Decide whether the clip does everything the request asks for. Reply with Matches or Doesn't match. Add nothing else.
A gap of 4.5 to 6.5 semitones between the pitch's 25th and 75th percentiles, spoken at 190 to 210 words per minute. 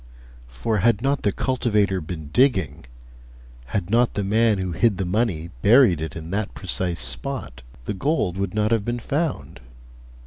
Doesn't match